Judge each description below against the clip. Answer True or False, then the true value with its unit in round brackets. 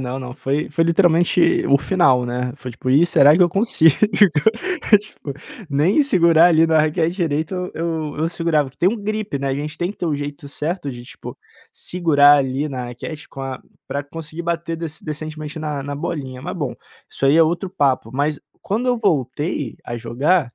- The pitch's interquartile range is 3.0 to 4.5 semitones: True (3.7 semitones)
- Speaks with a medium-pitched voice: True (155 Hz)